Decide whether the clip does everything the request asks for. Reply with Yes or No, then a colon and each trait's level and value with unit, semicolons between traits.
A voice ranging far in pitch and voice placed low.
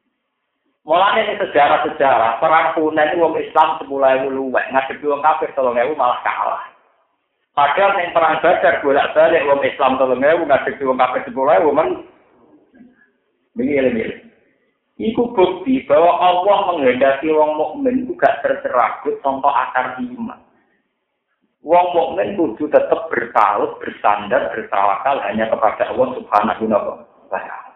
No: wide, 6.9 semitones; medium, 160 Hz